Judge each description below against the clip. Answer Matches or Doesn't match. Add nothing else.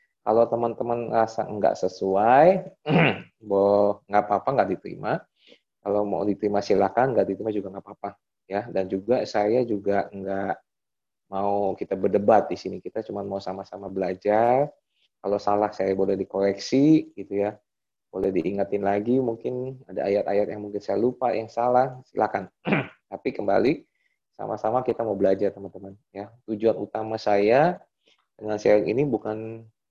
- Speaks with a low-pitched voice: Matches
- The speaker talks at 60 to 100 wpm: Doesn't match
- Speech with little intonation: Matches